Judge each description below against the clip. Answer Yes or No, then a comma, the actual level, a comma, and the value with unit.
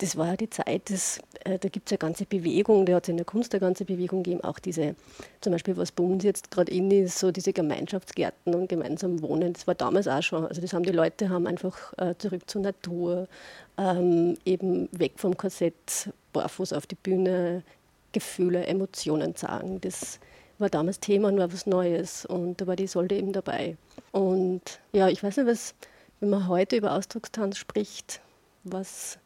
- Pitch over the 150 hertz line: Yes, medium, 185 Hz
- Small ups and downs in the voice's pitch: Yes, narrow, 1.9 semitones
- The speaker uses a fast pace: Yes, fast, 195 wpm